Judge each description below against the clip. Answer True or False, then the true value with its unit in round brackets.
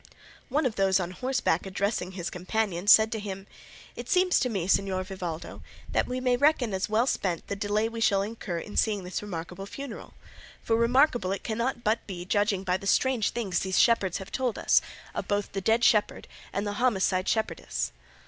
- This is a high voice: True (205 Hz)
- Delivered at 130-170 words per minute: False (190 wpm)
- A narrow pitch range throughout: False (3.6 semitones)